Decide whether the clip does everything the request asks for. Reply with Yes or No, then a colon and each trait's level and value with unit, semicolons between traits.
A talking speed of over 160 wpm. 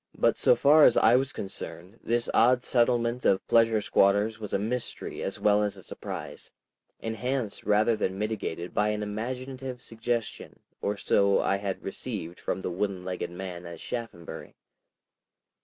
No: average, 155 wpm